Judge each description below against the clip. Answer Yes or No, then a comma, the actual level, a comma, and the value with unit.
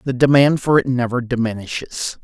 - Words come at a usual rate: Yes, average, 160 wpm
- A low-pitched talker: Yes, low, 125 Hz